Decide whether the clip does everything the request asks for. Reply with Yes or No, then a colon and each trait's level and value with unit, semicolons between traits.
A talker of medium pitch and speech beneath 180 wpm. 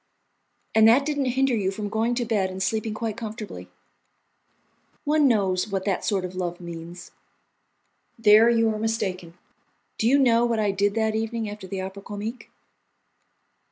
No: high, 215 Hz; average, 160 wpm